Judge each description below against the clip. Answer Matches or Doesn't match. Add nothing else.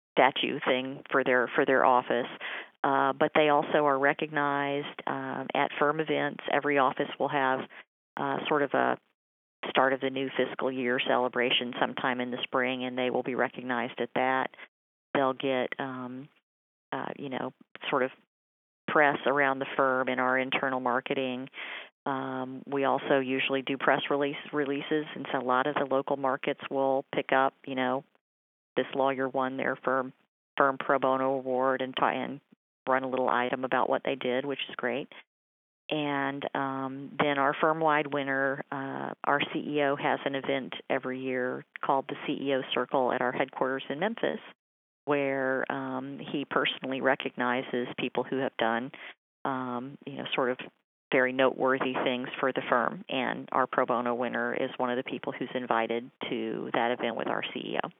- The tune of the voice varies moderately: Doesn't match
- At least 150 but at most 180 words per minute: Matches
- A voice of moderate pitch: Doesn't match